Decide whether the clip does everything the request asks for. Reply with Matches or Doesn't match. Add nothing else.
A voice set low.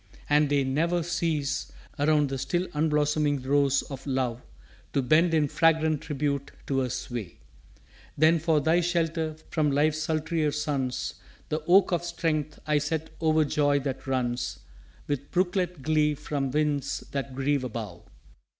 Doesn't match